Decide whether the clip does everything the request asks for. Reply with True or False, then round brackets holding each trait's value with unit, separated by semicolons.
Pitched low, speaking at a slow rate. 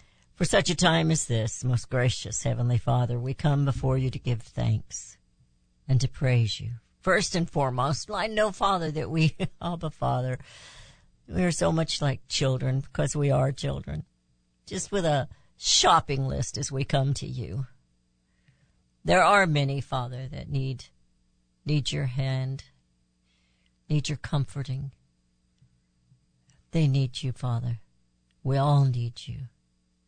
False (130 Hz; 145 wpm)